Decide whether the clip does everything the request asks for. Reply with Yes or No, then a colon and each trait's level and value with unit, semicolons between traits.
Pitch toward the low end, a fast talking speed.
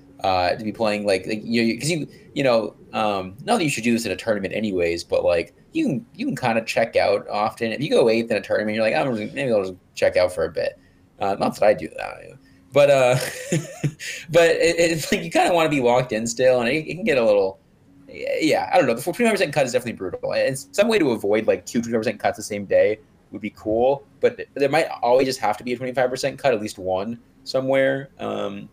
Yes: low, 130 Hz; fast, 260 wpm